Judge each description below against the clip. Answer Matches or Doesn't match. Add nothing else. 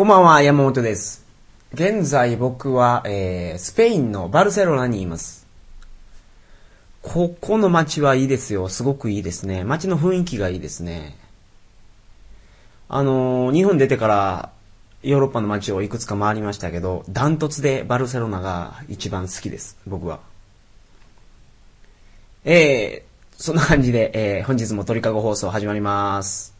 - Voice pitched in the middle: Doesn't match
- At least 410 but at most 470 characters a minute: Doesn't match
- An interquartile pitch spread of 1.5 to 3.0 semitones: Doesn't match